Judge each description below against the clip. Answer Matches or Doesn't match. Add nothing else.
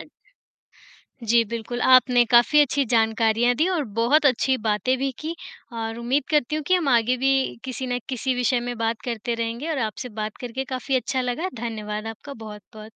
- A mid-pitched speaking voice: Doesn't match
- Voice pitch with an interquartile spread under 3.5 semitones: Matches